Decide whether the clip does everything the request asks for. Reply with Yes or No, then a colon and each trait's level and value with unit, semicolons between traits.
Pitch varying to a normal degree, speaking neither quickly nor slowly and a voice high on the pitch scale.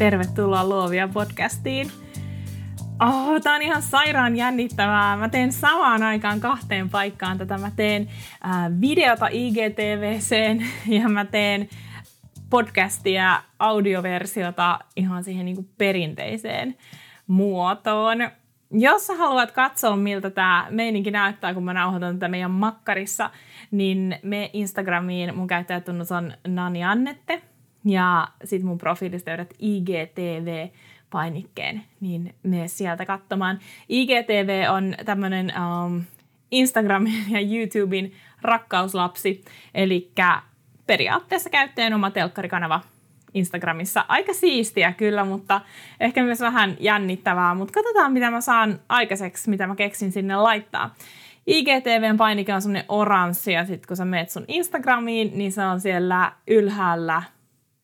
Yes: average, 3.6 semitones; average, 120 wpm; high, 195 Hz